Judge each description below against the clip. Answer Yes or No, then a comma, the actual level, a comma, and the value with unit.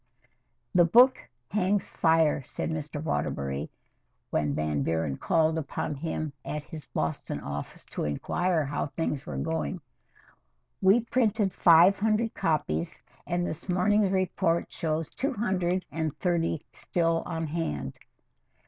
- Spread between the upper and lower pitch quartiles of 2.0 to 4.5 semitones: No, average, 5.0 semitones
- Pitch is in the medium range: Yes, medium, 165 Hz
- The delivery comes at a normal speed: No, slow, 130 wpm